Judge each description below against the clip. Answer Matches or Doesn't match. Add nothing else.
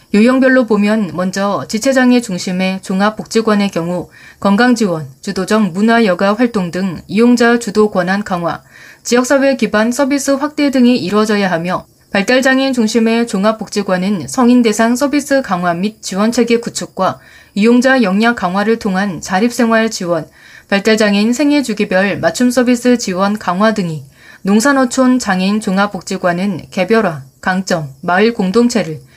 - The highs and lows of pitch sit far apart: Doesn't match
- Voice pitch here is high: Matches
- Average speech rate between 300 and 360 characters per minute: Matches